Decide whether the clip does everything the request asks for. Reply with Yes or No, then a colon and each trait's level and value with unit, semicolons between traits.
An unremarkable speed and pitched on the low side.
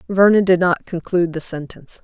No: average, 175 wpm; medium, 175 Hz